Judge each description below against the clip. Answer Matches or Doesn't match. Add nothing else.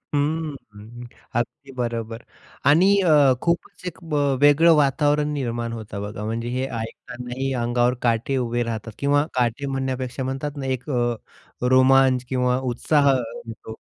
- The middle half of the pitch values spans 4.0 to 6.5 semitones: Doesn't match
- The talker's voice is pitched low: Matches